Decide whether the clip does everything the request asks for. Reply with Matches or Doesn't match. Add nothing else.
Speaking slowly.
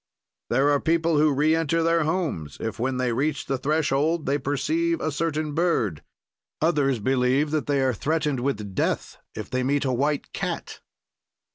Doesn't match